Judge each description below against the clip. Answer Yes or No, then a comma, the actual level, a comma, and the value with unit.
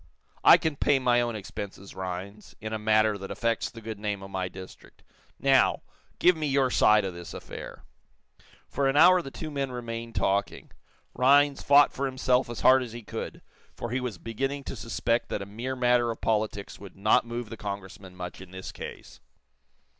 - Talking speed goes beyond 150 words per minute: Yes, average, 190 wpm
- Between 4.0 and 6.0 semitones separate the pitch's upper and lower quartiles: Yes, average, 4.4 semitones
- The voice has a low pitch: Yes, low, 115 Hz